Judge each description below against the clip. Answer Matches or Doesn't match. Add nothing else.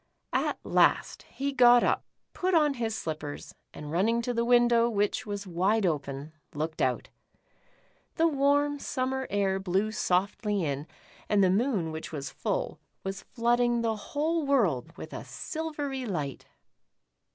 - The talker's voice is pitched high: Matches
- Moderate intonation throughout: Doesn't match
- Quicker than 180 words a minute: Doesn't match